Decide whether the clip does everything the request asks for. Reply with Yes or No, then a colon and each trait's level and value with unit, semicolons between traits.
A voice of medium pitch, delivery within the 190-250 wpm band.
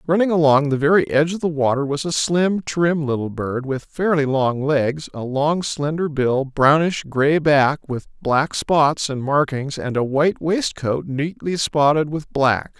No: medium, 145 Hz; average, 180 wpm